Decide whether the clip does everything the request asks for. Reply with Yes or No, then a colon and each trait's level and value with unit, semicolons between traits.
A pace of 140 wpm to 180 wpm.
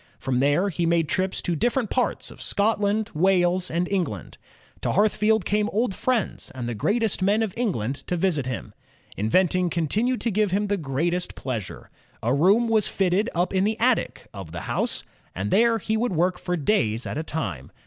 No: average, 190 wpm